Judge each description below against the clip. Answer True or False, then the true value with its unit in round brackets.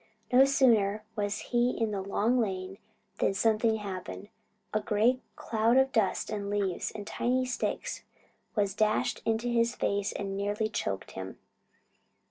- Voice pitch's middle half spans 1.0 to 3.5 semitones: True (2.7 semitones)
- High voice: True (215 Hz)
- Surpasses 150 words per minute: False (145 wpm)